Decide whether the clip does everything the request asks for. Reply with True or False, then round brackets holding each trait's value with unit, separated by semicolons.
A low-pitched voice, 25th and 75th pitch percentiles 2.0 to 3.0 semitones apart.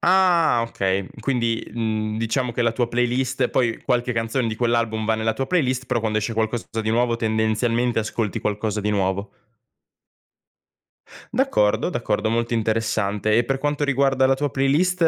True (115 Hz; 2.7 semitones)